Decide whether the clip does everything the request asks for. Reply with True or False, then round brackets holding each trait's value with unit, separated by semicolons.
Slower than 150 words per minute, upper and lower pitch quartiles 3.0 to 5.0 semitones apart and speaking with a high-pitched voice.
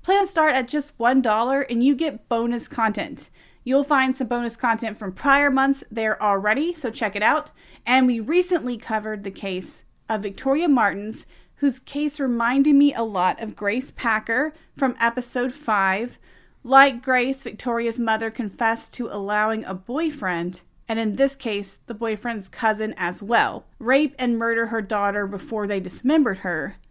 False (160 wpm; 3.9 semitones; 235 Hz)